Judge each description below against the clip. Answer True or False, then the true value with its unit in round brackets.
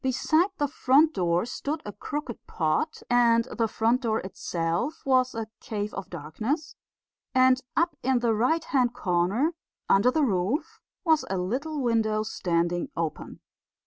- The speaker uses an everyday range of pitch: False (6.4 semitones)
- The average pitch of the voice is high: True (235 Hz)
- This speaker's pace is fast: False (145 wpm)